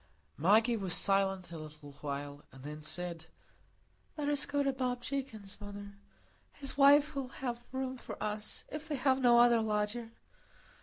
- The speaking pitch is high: Yes, high, 220 Hz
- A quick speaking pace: No, average, 160 wpm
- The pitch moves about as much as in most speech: No, wide, 6.3 semitones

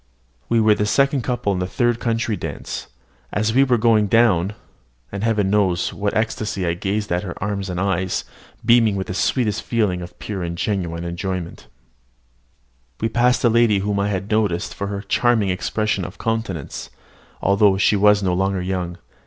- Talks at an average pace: Yes, average, 180 wpm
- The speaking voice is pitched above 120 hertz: No, low, 100 Hz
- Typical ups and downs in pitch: Yes, average, 3.0 semitones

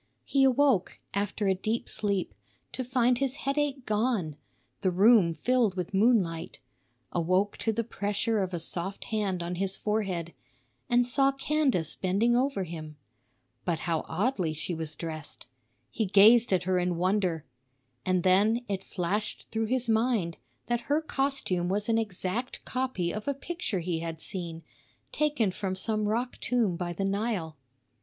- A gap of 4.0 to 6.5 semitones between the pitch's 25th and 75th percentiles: Yes, average, 5.1 semitones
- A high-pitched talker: Yes, high, 205 Hz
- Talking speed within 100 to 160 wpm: Yes, average, 155 wpm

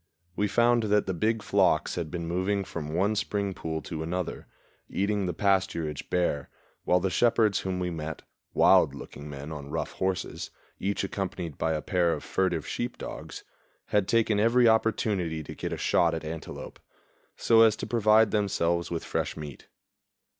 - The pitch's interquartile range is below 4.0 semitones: No, average, 4.3 semitones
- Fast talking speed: No, average, 170 wpm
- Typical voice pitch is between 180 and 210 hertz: No, very low, 95 Hz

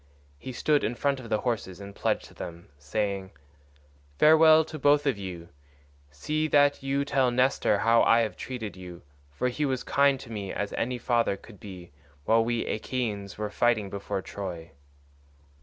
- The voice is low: Yes, low, 115 Hz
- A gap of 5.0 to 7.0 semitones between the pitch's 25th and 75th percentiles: Yes, average, 5.3 semitones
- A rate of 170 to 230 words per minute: Yes, average, 175 wpm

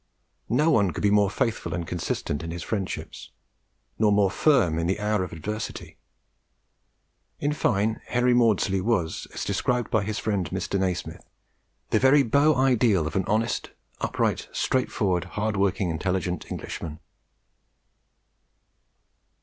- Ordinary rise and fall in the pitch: Yes, average, 4.0 semitones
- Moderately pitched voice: No, low, 100 Hz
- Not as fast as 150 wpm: Yes, average, 140 wpm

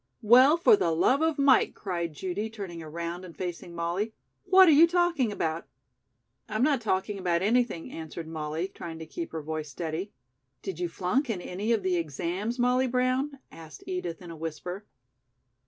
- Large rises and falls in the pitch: Yes, wide, 6.8 semitones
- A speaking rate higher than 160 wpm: Yes, average, 175 wpm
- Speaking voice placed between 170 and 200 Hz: Yes, medium, 185 Hz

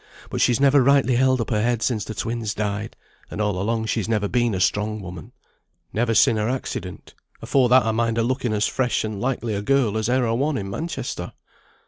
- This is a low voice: Yes, low, 115 Hz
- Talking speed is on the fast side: Yes, fast, 220 wpm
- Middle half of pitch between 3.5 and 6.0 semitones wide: No, average, 2.9 semitones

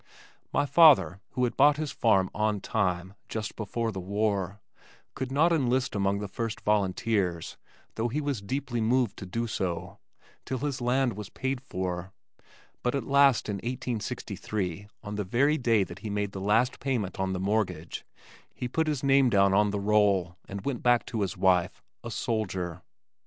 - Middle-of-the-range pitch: No, low, 105 Hz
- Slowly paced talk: No, average, 175 wpm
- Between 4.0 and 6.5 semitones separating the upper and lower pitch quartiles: Yes, average, 4.6 semitones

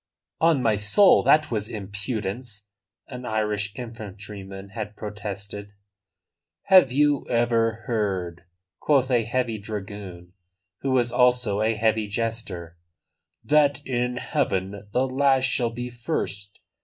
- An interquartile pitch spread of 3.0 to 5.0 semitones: Yes, average, 3.5 semitones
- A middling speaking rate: No, slow, 120 wpm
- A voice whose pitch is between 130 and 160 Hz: No, low, 110 Hz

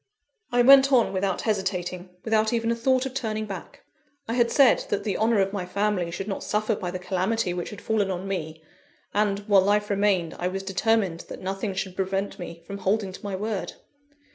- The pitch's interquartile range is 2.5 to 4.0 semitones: Yes, average, 2.8 semitones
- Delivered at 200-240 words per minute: Yes, fast, 205 wpm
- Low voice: No, high, 200 Hz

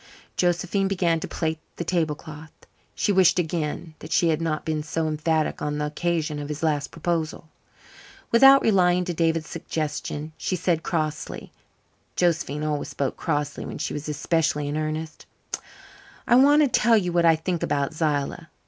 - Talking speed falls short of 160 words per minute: No, average, 165 wpm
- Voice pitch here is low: No, medium, 160 Hz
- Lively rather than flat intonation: No, narrow, 2.5 semitones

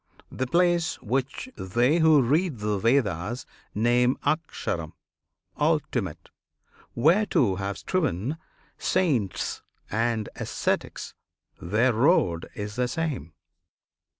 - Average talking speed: No, slow, 95 wpm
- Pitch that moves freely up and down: Yes, wide, 7.1 semitones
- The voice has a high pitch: No, low, 125 Hz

